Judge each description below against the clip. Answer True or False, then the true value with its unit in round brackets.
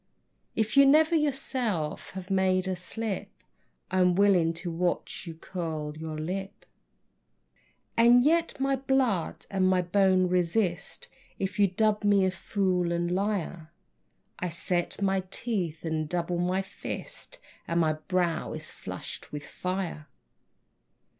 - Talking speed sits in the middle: False (130 wpm)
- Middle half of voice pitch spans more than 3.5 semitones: False (3.1 semitones)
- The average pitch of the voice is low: False (185 Hz)